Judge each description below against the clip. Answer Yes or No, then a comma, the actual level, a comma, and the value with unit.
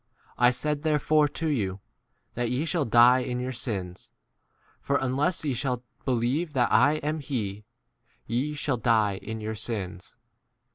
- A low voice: Yes, low, 125 Hz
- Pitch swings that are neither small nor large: Yes, average, 4.7 semitones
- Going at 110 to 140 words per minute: No, average, 160 wpm